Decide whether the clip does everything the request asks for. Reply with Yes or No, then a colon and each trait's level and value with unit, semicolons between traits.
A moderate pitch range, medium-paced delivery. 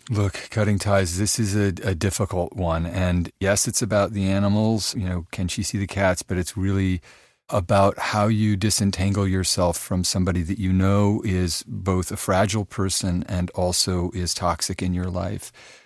No: narrow, 2.2 semitones; average, 180 wpm